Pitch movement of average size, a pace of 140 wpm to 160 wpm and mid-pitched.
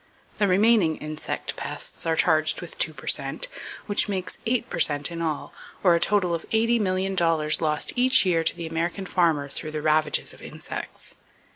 No: average, 4.1 semitones; average, 175 wpm; medium, 170 Hz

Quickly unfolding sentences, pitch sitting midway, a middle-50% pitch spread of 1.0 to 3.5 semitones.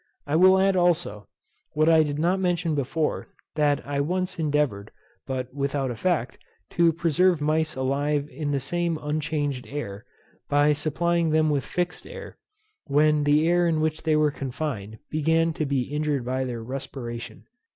No: average, 160 wpm; medium, 150 Hz; average, 2.9 semitones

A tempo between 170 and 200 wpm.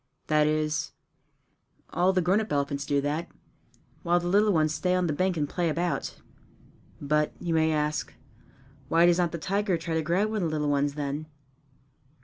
Yes: average, 185 wpm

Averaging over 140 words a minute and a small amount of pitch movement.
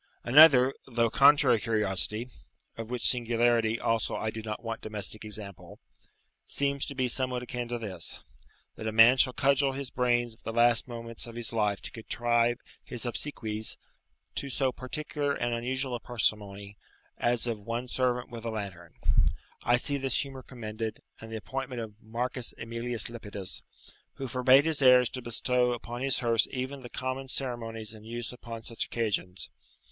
Yes: average, 165 wpm; narrow, 2.3 semitones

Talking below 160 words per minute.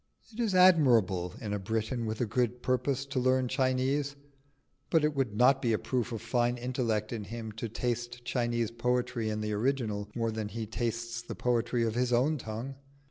No: average, 190 wpm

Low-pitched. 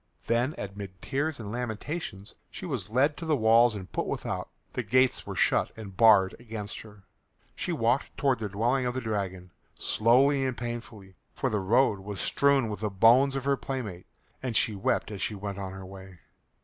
Yes: low, 115 Hz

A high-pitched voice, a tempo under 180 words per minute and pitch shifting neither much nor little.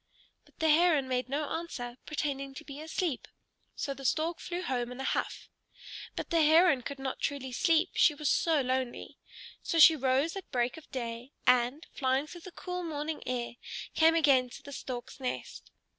No: very high, 285 Hz; average, 185 wpm; average, 3.8 semitones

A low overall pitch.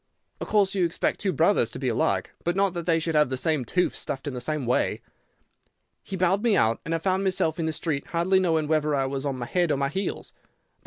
No: medium, 160 Hz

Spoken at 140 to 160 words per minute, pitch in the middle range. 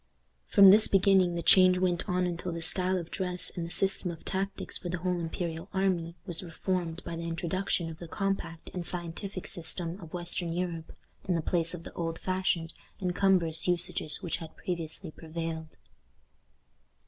No: average, 175 wpm; medium, 175 Hz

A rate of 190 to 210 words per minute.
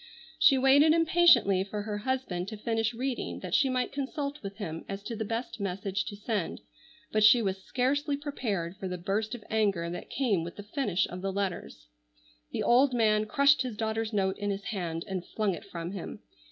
Yes: average, 200 wpm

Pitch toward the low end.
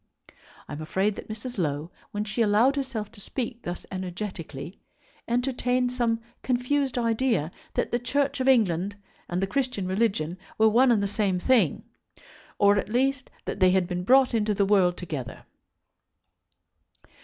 No: high, 215 Hz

